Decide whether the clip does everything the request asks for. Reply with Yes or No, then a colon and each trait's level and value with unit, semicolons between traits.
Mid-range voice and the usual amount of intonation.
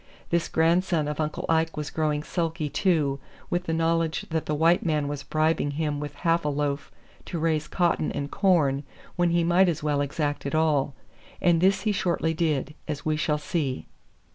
No: medium, 155 Hz; narrow, 2.3 semitones